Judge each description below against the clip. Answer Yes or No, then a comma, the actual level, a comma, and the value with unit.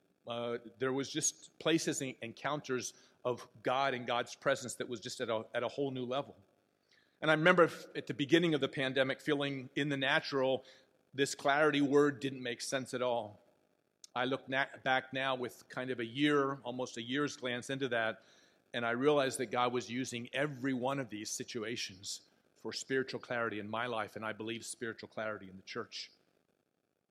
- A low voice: Yes, low, 130 Hz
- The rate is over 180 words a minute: Yes, average, 190 wpm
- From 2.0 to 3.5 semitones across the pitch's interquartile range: Yes, average, 2.7 semitones